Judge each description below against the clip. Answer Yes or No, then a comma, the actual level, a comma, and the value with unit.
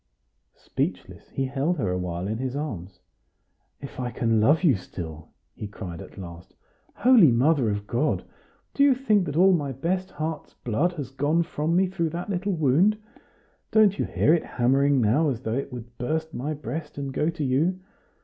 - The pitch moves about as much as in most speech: No, wide, 6.1 semitones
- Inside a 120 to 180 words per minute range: No, average, 190 wpm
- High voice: No, medium, 145 Hz